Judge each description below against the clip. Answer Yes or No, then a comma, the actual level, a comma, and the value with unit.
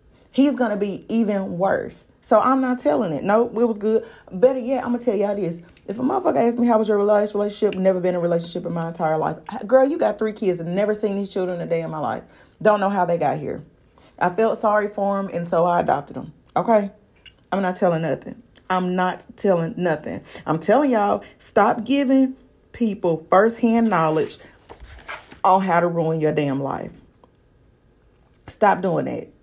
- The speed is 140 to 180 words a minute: No, average, 200 wpm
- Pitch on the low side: No, high, 200 Hz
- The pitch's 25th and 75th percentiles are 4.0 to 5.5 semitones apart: Yes, average, 4.7 semitones